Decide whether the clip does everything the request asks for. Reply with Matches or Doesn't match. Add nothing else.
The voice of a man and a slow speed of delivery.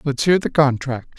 Doesn't match